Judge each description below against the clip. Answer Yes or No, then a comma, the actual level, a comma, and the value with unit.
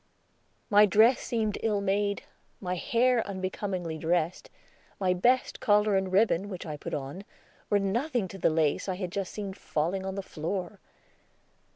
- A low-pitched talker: No, high, 195 Hz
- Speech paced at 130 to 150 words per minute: No, average, 160 wpm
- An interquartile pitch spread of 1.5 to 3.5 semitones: Yes, narrow, 2.5 semitones